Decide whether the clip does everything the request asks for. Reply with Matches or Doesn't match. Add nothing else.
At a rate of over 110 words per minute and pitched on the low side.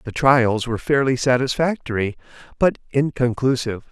Doesn't match